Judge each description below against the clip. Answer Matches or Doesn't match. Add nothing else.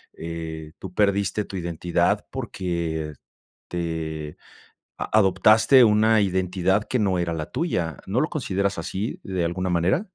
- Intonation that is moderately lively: Matches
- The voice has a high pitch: Doesn't match